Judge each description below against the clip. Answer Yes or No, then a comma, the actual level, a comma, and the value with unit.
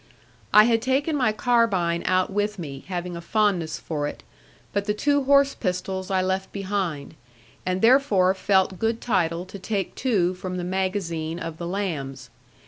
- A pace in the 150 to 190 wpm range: Yes, average, 165 wpm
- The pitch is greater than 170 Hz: Yes, high, 190 Hz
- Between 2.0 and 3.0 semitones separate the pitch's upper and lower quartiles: No, average, 3.5 semitones